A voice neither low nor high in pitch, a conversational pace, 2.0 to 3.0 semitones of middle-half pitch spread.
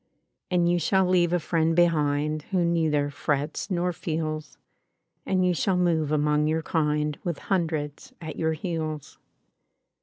Yes: medium, 160 Hz; average, 150 wpm; narrow, 2.5 semitones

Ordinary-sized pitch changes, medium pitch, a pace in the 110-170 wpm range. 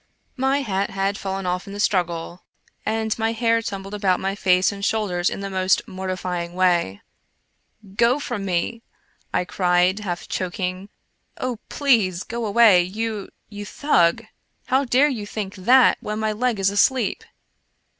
No: average, 3.5 semitones; high, 200 Hz; average, 165 wpm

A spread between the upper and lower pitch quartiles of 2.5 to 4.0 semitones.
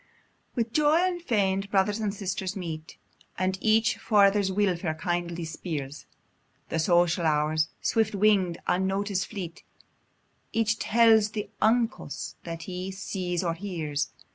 Yes: average, 3.7 semitones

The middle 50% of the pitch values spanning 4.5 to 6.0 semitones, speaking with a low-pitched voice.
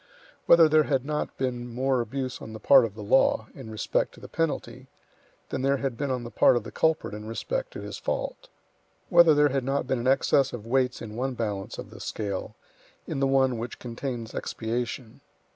No: average, 3.2 semitones; low, 130 Hz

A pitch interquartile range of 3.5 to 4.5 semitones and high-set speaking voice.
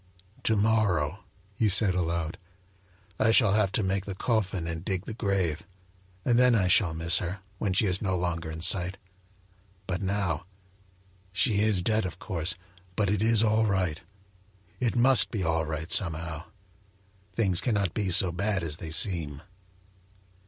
No: average, 4.0 semitones; very low, 95 Hz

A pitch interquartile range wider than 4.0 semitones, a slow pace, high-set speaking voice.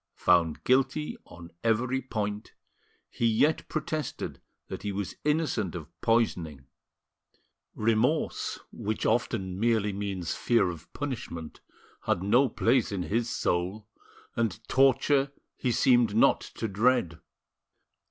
No: average, 5.0 semitones; slow, 115 wpm; low, 110 Hz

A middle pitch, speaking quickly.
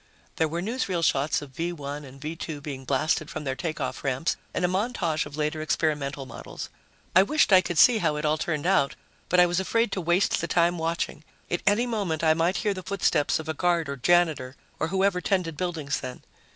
Yes: medium, 165 Hz; fast, 215 wpm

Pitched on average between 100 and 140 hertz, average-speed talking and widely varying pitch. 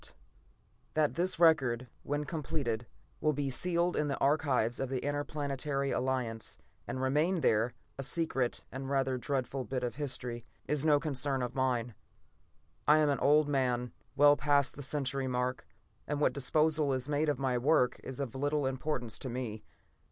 No: low, 135 Hz; average, 165 wpm; narrow, 2.6 semitones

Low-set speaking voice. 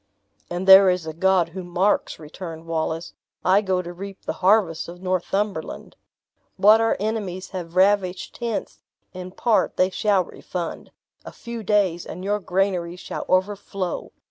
No: medium, 185 Hz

